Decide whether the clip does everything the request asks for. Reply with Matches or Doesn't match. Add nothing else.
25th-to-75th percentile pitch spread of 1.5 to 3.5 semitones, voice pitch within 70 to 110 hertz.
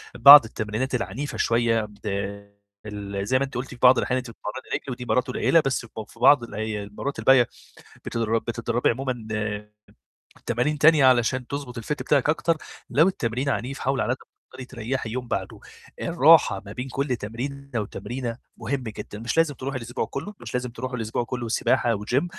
Doesn't match